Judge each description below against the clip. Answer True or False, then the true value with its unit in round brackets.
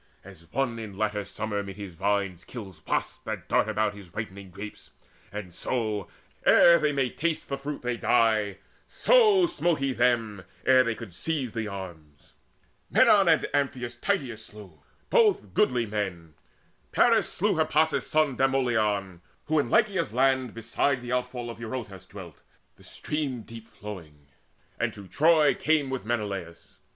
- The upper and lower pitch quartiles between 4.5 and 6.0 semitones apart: True (5.1 semitones)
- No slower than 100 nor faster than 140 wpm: False (155 wpm)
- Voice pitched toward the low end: True (115 Hz)